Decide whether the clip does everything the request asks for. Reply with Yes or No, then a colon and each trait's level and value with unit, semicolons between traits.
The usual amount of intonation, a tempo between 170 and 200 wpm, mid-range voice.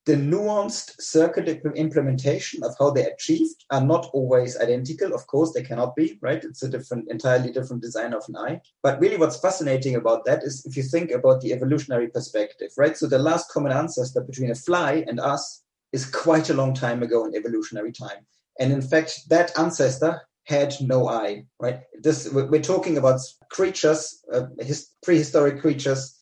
Yes: average, 4.0 semitones; average, 180 wpm; medium, 145 Hz